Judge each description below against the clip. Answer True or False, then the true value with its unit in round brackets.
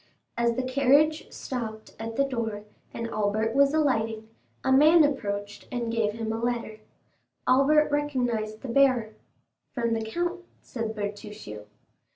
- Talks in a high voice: True (235 Hz)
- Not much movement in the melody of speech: False (4.0 semitones)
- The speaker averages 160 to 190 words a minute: False (140 wpm)